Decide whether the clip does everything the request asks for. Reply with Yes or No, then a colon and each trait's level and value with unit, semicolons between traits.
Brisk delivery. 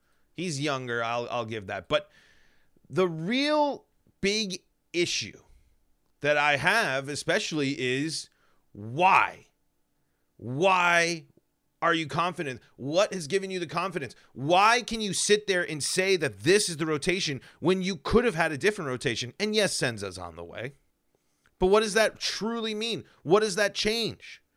No: average, 155 wpm